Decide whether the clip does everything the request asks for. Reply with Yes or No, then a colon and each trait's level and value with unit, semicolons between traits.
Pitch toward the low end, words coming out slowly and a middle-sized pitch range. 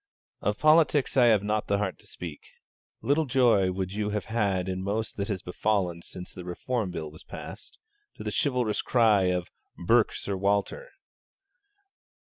No: low, 100 Hz; average, 165 wpm; average, 4.1 semitones